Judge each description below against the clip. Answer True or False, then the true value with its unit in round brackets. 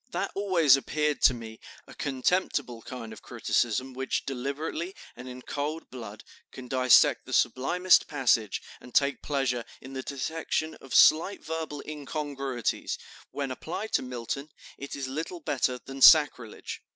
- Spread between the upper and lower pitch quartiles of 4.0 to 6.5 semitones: False (3.4 semitones)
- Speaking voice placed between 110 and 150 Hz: True (135 Hz)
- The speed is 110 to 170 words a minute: True (145 wpm)